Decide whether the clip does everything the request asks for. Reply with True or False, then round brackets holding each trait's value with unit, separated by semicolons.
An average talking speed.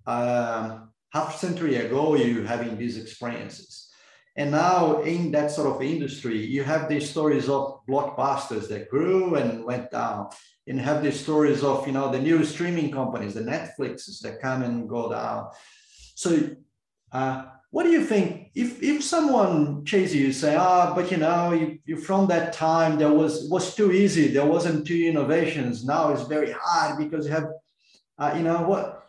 True (180 wpm)